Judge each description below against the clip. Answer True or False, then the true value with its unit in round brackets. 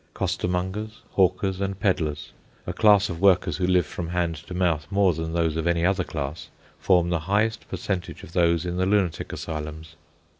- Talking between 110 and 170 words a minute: False (180 wpm)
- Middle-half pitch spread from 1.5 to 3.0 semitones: True (2.7 semitones)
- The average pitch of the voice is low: True (90 Hz)